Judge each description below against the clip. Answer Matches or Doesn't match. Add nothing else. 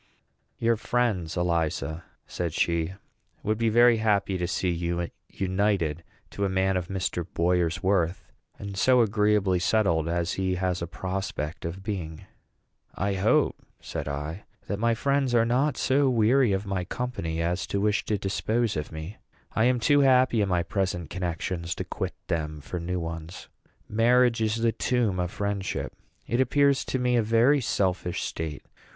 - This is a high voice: Doesn't match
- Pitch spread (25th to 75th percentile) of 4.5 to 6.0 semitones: Matches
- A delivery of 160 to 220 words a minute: Matches